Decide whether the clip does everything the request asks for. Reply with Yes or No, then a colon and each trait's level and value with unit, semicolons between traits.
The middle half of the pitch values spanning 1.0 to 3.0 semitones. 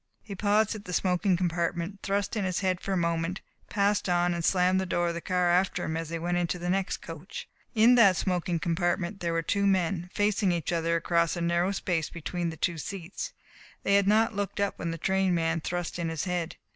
Yes: narrow, 2.5 semitones